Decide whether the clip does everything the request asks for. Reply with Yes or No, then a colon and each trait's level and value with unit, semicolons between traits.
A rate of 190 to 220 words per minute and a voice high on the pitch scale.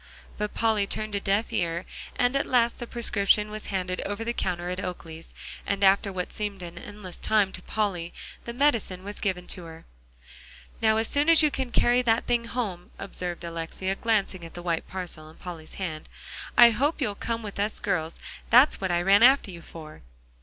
Yes: average, 195 wpm; high, 200 Hz